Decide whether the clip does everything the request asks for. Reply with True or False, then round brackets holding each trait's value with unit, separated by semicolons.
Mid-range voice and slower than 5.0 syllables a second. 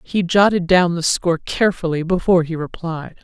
False (175 Hz; 5.5 syllables/s)